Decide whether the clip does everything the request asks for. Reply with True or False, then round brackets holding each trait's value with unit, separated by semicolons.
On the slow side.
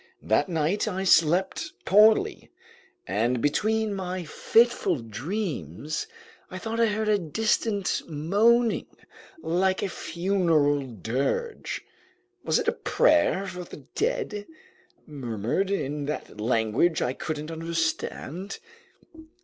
True (110 wpm)